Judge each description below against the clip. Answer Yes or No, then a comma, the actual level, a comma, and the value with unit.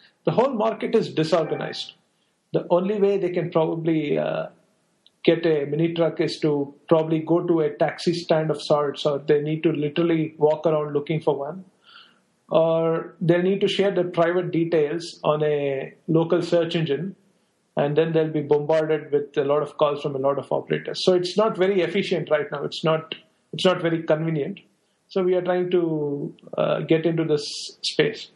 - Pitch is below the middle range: No, medium, 165 Hz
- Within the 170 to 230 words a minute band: Yes, average, 185 wpm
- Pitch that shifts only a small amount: No, average, 3.0 semitones